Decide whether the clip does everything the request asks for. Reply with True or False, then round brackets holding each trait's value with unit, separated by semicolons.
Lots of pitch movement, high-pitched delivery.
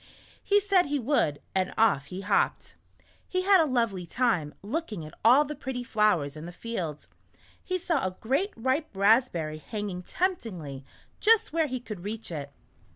True (8.9 semitones; 225 Hz)